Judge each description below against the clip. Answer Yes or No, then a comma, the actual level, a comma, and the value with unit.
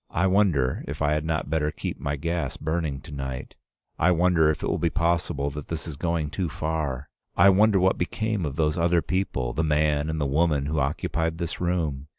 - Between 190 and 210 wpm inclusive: Yes, fast, 205 wpm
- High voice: No, very low, 80 Hz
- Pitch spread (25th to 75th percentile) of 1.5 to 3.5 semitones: Yes, average, 3.0 semitones